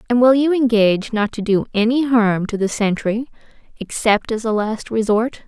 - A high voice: Yes, high, 225 Hz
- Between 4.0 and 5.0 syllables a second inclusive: Yes, 4.9 syllables/s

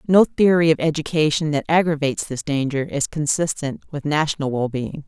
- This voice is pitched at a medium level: Yes, medium, 150 Hz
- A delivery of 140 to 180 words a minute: Yes, average, 155 wpm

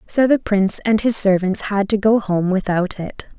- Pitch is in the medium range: No, high, 205 Hz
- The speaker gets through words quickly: Yes, fast, 215 wpm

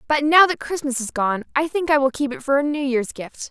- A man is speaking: No, female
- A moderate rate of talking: No, fast, 290 wpm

